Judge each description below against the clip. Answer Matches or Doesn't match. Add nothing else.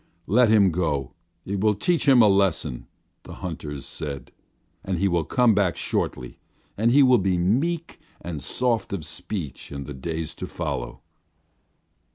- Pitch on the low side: Matches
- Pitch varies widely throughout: Matches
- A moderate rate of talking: Matches